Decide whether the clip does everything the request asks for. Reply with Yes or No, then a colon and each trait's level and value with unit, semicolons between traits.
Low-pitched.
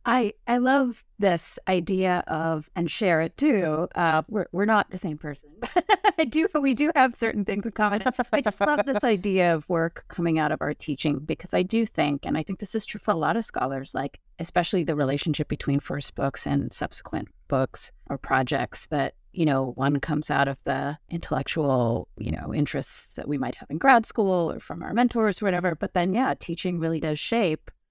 No: medium, 175 Hz